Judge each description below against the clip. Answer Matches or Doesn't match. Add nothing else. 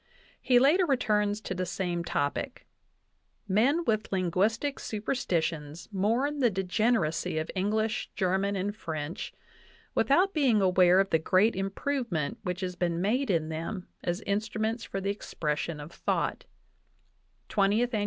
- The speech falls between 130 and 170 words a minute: Matches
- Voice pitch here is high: Matches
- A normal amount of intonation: Matches